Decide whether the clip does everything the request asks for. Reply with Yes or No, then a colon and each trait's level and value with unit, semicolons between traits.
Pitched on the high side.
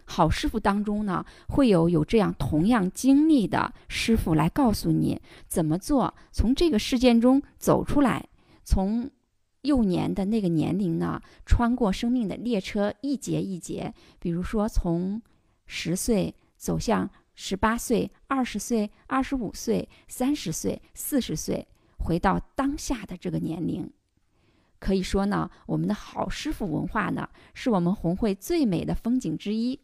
Yes: high, 210 Hz